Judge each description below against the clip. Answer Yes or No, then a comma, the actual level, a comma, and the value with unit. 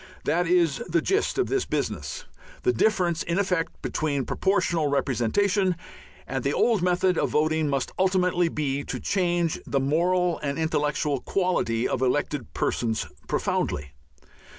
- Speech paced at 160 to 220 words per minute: No, average, 140 wpm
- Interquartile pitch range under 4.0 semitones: No, average, 4.3 semitones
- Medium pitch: Yes, medium, 165 Hz